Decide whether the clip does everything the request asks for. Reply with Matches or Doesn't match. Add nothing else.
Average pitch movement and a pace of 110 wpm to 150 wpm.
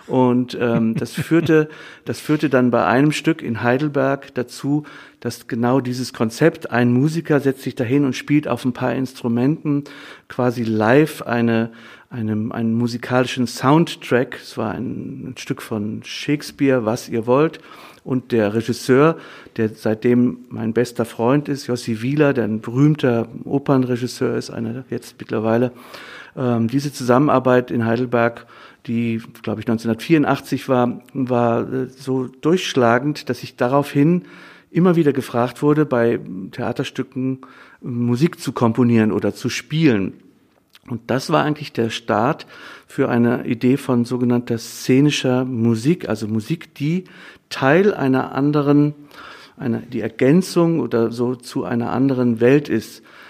Matches